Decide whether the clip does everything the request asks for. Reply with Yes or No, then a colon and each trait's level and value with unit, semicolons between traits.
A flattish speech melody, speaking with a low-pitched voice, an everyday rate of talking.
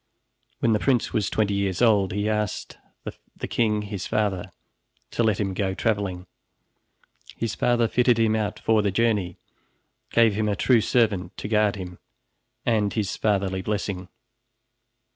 Yes: narrow, 2.3 semitones; low, 105 Hz; average, 150 wpm